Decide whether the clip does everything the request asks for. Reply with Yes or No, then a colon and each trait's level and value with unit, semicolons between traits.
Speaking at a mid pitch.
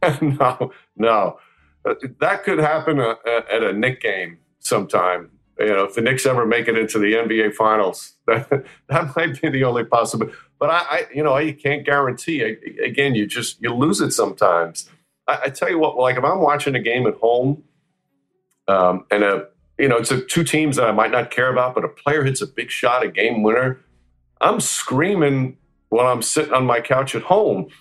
No: low, 130 Hz